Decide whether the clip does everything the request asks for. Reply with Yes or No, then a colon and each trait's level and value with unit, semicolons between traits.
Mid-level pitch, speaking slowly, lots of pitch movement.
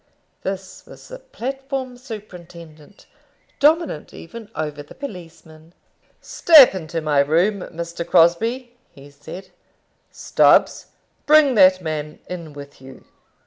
Yes: medium, 180 Hz; slow, 110 wpm; wide, 7.6 semitones